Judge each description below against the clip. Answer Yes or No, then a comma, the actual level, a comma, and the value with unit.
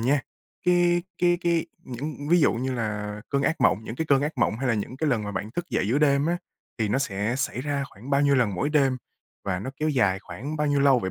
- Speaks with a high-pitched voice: No, low, 135 Hz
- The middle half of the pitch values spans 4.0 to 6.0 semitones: Yes, average, 5.1 semitones